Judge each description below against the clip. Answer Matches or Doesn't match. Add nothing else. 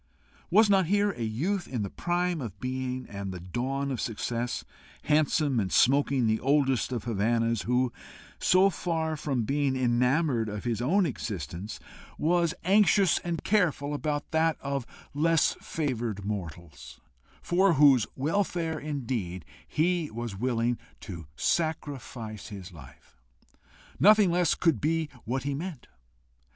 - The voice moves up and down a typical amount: Doesn't match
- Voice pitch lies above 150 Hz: Doesn't match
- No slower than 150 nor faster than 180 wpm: Doesn't match